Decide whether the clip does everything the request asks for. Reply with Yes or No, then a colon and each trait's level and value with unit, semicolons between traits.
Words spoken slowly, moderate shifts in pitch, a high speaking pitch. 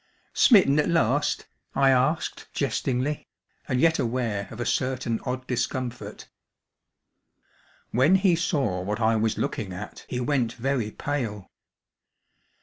No: slow, 125 wpm; average, 3.9 semitones; low, 125 Hz